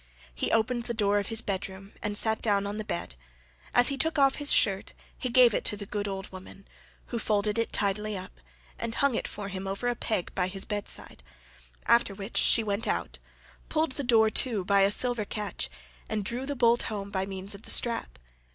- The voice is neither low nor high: No, high, 210 Hz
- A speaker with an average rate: No, fast, 220 wpm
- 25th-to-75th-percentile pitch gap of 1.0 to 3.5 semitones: Yes, average, 3.1 semitones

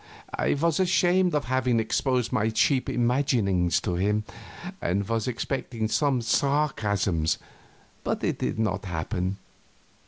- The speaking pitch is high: No, low, 115 Hz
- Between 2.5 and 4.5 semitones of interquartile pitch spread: No, wide, 5.5 semitones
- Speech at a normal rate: No, slow, 125 wpm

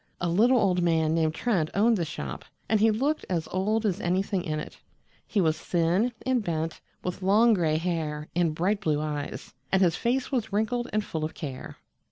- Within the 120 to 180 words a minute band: No, average, 200 wpm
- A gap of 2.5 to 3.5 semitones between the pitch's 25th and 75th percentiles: No, average, 5.0 semitones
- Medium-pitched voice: Yes, medium, 180 Hz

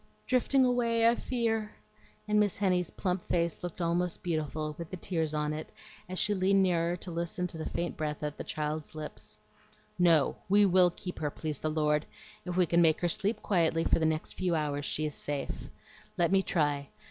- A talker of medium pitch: Yes, medium, 170 Hz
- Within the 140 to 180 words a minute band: No, average, 200 wpm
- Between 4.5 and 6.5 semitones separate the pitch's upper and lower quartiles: No, average, 3.4 semitones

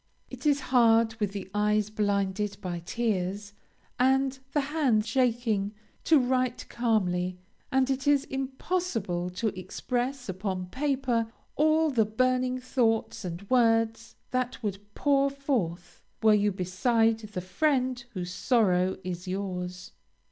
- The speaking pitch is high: Yes, high, 225 Hz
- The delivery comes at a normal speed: No, slow, 125 wpm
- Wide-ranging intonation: No, average, 5.0 semitones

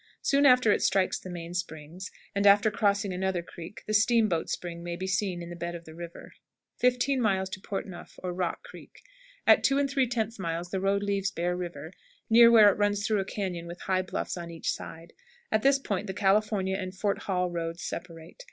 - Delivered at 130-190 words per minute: No, fast, 205 wpm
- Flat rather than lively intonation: No, average, 3.4 semitones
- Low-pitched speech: No, high, 190 Hz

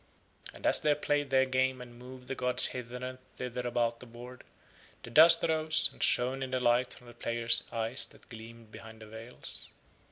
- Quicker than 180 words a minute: Yes, average, 195 wpm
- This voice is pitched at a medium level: No, low, 125 Hz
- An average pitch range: No, narrow, 1.9 semitones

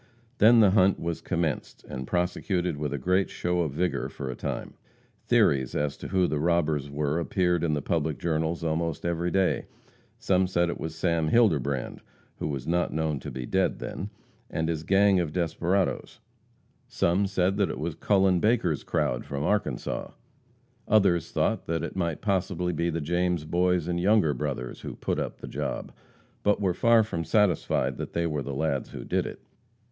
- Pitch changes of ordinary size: Yes, average, 3.3 semitones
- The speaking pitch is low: Yes, very low, 85 Hz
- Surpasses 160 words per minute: Yes, average, 180 wpm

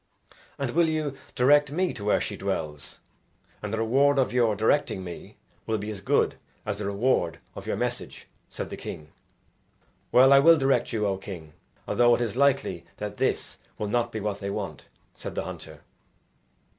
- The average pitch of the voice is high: No, low, 115 Hz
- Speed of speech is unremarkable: Yes, average, 180 wpm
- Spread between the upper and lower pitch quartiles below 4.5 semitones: No, average, 5.2 semitones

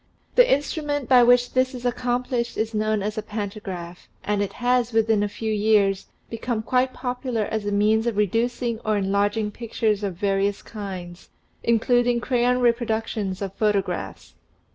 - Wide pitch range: No, average, 3.1 semitones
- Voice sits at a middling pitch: No, high, 220 Hz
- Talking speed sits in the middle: Yes, average, 155 wpm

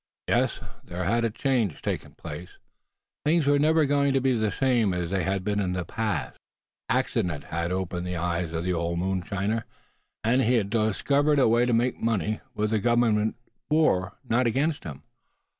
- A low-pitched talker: Yes, low, 110 Hz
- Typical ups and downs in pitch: No, wide, 5.7 semitones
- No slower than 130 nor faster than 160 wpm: No, average, 180 wpm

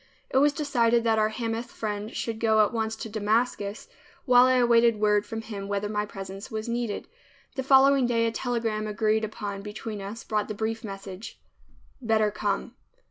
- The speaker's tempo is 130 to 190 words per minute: Yes, average, 180 wpm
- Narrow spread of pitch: Yes, narrow, 2.1 semitones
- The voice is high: Yes, high, 220 Hz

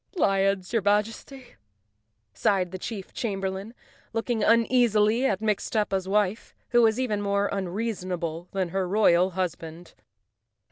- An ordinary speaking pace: No, slow, 125 wpm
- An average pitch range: Yes, average, 3.0 semitones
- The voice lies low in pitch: No, high, 200 Hz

